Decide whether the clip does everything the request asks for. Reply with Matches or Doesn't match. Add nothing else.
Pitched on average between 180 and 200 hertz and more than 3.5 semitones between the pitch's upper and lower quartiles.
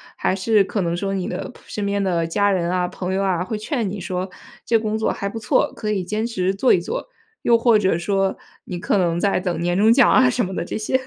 Doesn't match